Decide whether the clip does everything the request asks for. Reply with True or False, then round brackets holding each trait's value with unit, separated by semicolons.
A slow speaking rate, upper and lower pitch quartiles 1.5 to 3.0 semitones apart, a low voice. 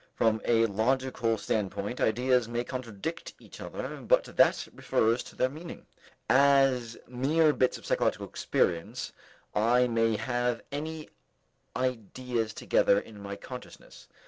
True (125 wpm; 2.7 semitones; 120 Hz)